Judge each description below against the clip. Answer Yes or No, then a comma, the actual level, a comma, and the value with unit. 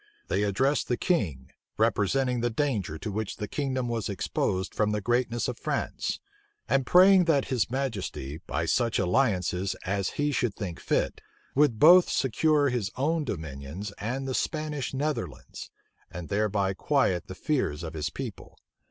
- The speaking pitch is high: No, low, 115 Hz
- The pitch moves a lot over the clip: Yes, wide, 6.3 semitones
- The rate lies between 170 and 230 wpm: No, average, 155 wpm